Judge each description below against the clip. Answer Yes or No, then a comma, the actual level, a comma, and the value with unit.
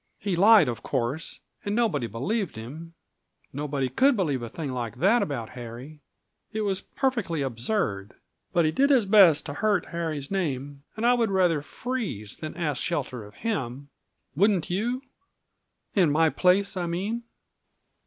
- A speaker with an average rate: Yes, average, 155 wpm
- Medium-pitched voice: Yes, medium, 165 Hz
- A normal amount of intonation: No, wide, 7.2 semitones